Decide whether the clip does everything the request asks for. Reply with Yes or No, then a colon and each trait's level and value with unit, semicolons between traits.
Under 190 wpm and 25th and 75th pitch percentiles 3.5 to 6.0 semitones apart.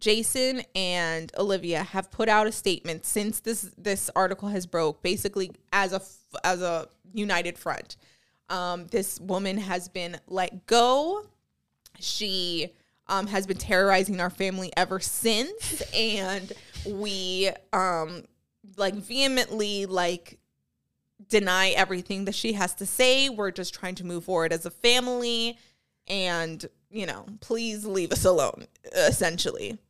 No: slow, 135 wpm; average, 2.9 semitones